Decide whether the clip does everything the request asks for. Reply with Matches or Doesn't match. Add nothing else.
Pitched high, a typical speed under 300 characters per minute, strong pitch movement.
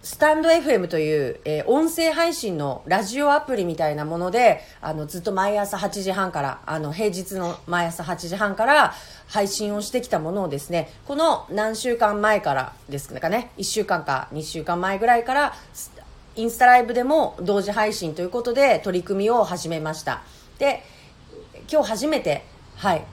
Doesn't match